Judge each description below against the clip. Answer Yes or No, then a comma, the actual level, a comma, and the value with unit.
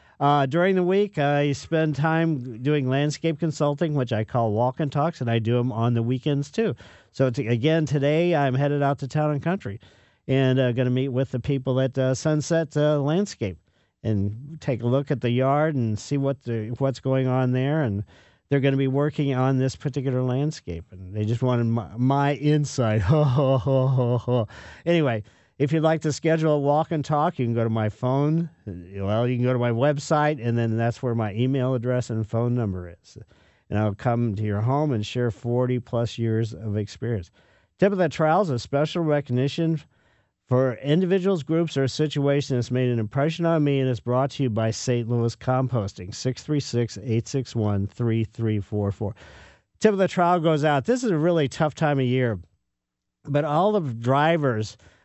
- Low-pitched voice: Yes, low, 130 Hz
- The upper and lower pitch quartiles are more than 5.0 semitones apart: No, average, 4.3 semitones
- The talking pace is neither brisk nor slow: Yes, average, 190 wpm